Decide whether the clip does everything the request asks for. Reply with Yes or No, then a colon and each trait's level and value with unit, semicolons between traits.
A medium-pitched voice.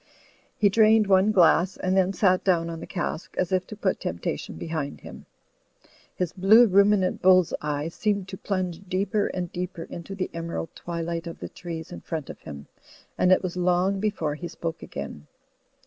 Yes: medium, 180 Hz